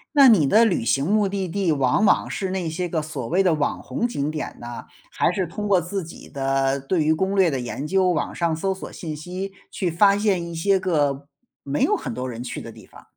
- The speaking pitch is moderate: Yes, medium, 170 Hz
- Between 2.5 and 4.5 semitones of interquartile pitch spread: No, average, 4.9 semitones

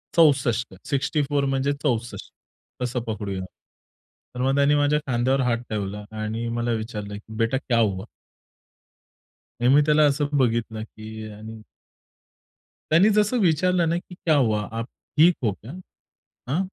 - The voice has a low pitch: Yes, low, 125 Hz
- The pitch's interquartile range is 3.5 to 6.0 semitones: Yes, average, 4.9 semitones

